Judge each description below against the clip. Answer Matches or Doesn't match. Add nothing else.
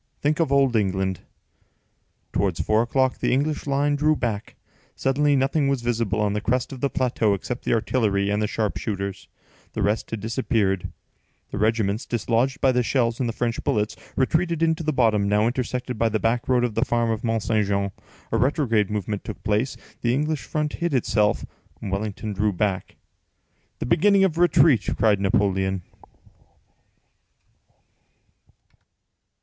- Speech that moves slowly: Doesn't match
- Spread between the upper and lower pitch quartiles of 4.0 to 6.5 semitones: Matches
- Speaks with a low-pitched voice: Matches